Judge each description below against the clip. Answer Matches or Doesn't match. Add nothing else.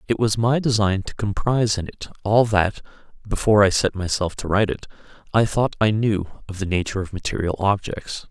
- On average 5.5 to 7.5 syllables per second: Matches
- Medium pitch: Doesn't match